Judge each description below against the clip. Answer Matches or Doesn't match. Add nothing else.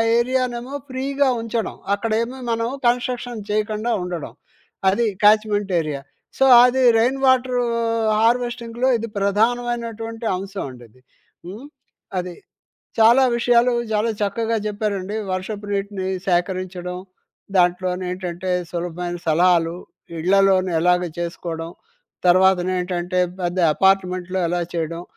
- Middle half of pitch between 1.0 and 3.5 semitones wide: Doesn't match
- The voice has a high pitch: Matches